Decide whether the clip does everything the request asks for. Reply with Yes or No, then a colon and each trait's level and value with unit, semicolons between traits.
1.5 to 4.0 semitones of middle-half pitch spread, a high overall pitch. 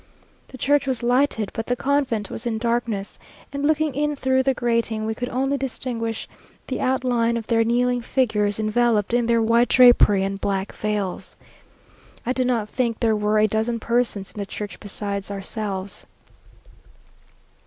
Yes: average, 3.0 semitones; high, 230 Hz